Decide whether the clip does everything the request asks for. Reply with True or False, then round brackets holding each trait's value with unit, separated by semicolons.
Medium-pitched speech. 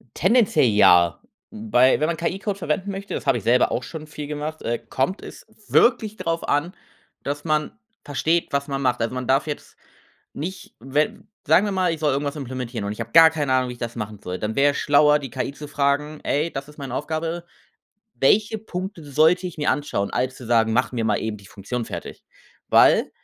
True (145 Hz)